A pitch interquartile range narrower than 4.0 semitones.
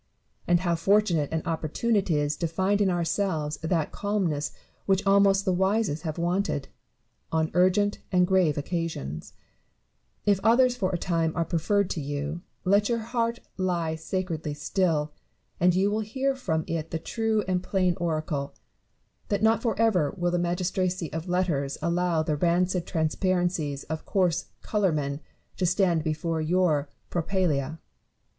Yes: average, 3.6 semitones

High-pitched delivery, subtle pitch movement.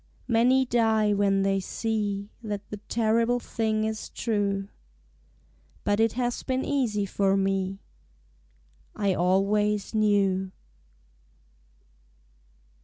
Yes: high, 210 Hz; narrow, 2.3 semitones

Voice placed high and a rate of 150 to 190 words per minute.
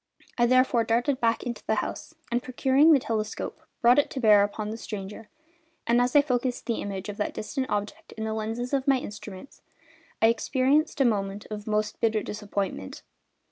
Yes: high, 230 Hz; average, 185 wpm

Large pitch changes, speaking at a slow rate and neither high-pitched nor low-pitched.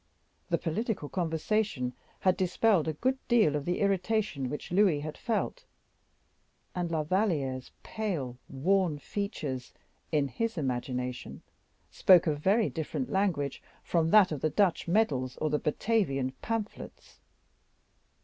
Yes: wide, 6.0 semitones; slow, 130 wpm; medium, 170 Hz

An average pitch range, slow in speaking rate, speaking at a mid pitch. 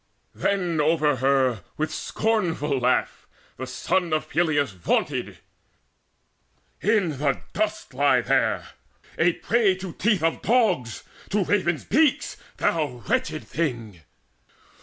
No: wide, 6.4 semitones; slow, 115 wpm; medium, 160 Hz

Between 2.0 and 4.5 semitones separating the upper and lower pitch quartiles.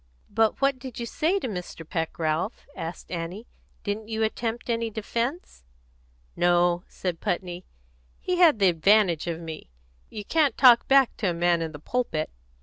No: wide, 5.6 semitones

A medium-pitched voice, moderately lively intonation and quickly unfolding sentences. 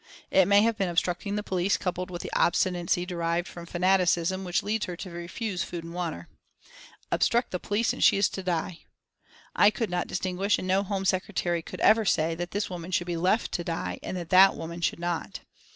No: medium, 180 Hz; narrow, 2.0 semitones; fast, 210 wpm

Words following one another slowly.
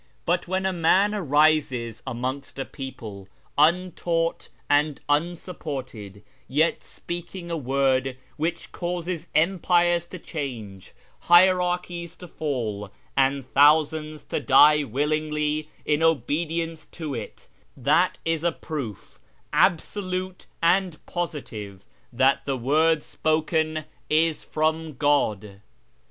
Yes: slow, 105 wpm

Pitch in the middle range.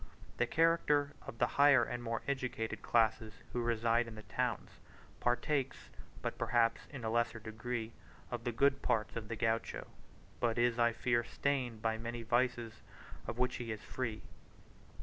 No: low, 120 Hz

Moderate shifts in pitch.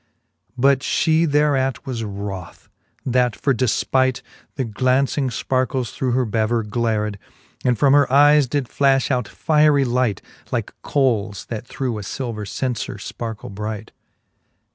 Yes: average, 3.6 semitones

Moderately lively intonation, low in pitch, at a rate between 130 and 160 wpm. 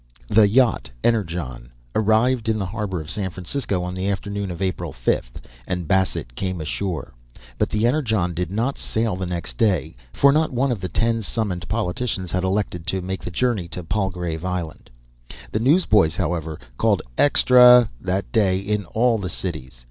No: average, 4.1 semitones; very low, 95 Hz; average, 170 wpm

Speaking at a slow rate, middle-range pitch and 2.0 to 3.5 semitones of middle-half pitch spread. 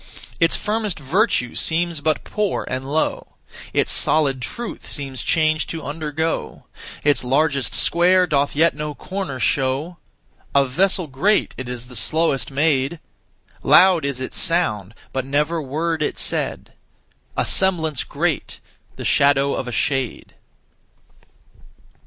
No: slow, 130 wpm; medium, 150 Hz; average, 3.9 semitones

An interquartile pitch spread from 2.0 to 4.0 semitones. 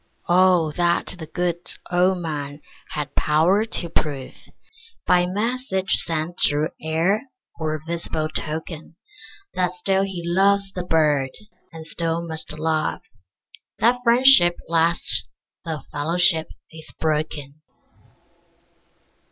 Yes: average, 2.9 semitones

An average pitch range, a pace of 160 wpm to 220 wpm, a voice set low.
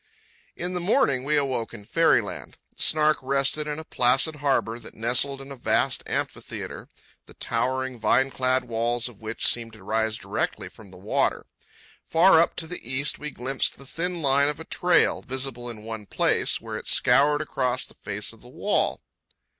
Yes: average, 4.0 semitones; average, 185 wpm; low, 130 Hz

